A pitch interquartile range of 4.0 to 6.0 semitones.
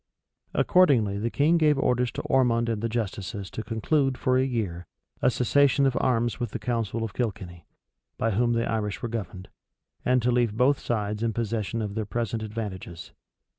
No: average, 3.0 semitones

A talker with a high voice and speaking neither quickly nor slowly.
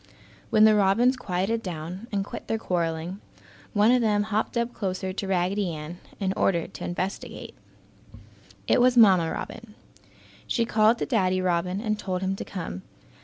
Yes: high, 195 Hz; average, 165 wpm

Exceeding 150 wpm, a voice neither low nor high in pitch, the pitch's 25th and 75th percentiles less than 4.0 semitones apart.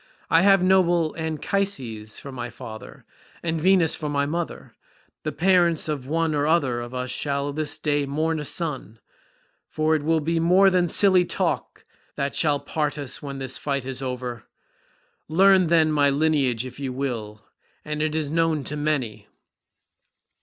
Yes: average, 160 wpm; medium, 150 Hz; average, 3.4 semitones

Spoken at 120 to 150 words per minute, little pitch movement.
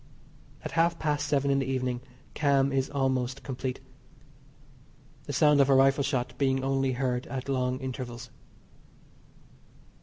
Yes: average, 140 wpm; narrow, 1.4 semitones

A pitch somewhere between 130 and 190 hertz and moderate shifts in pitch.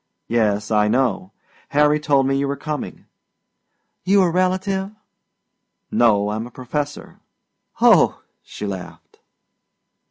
No: low, 135 Hz; wide, 6.0 semitones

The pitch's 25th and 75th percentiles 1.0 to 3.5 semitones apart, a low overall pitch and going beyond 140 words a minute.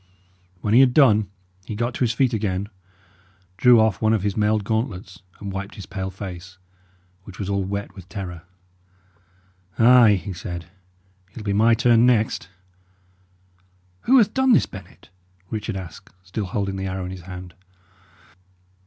Yes: average, 3.1 semitones; low, 100 Hz; average, 160 wpm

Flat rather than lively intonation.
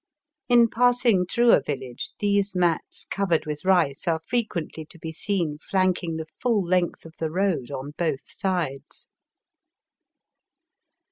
No: average, 4.2 semitones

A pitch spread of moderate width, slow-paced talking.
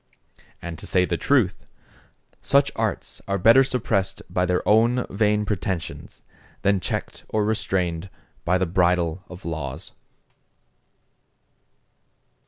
Yes: average, 3.3 semitones; slow, 115 wpm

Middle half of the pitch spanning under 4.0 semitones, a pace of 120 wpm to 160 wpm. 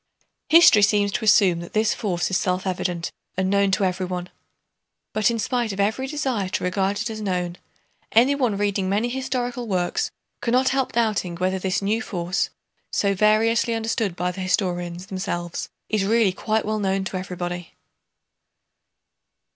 Yes: average, 3.5 semitones; average, 155 wpm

